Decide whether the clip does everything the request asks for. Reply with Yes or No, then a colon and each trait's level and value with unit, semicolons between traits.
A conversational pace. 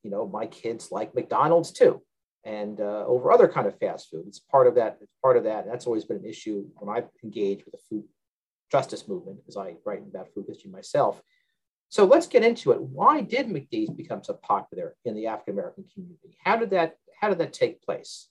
No: fast, 215 wpm